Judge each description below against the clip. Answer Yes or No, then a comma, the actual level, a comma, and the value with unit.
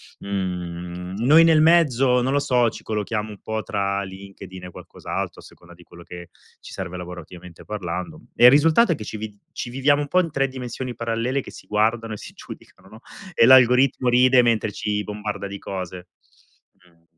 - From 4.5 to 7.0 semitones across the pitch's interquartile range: Yes, wide, 5.4 semitones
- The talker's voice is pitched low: Yes, low, 110 Hz